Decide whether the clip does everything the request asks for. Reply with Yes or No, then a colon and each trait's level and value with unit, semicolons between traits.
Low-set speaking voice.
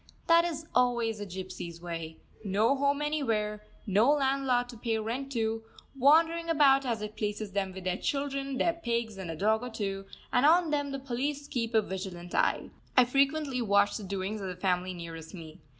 No: high, 225 Hz